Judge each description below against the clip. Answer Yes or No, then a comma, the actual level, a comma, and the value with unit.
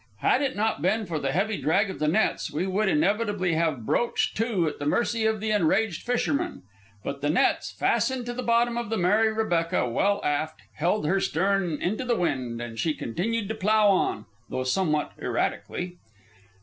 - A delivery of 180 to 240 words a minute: Yes, average, 190 wpm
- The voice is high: Yes, high, 195 Hz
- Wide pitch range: Yes, wide, 5.8 semitones